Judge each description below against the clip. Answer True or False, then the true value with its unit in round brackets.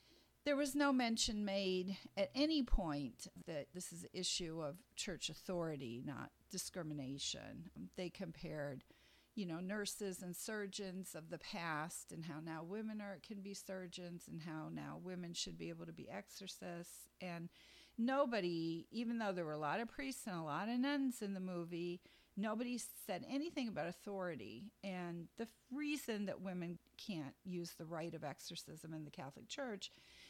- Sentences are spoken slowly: False (170 wpm)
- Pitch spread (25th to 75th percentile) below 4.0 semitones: False (4.5 semitones)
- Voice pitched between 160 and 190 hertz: True (185 Hz)